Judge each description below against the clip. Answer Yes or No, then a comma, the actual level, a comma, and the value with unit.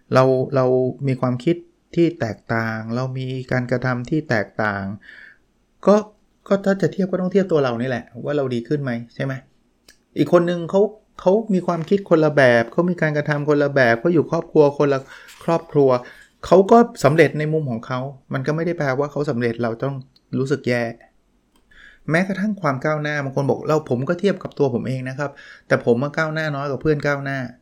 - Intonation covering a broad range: No, average, 4.6 semitones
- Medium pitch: Yes, medium, 145 Hz